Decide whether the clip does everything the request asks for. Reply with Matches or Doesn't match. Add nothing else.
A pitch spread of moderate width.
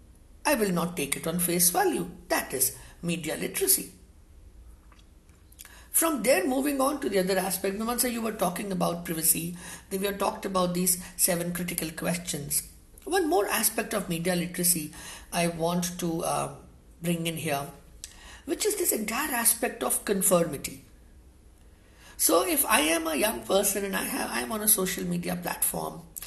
Doesn't match